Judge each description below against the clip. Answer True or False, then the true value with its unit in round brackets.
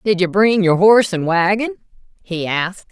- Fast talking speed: False (185 wpm)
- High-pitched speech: True (195 Hz)